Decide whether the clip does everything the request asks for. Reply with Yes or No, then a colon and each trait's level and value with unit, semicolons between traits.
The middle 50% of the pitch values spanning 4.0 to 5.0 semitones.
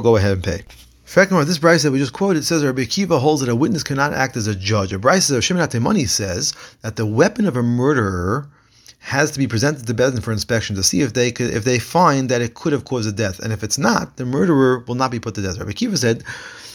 Yes: average, 4.6 semitones